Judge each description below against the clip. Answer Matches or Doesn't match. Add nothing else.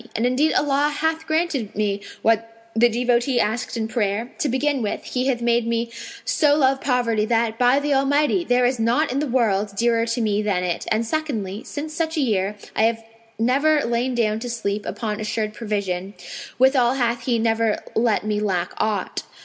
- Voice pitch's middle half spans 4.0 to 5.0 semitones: Doesn't match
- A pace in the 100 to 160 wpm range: Doesn't match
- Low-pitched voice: Doesn't match